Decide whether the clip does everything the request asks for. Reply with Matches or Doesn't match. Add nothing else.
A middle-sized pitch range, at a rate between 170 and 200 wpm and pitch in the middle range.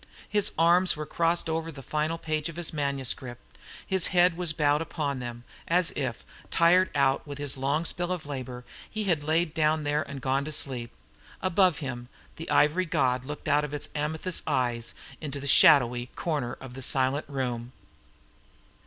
Matches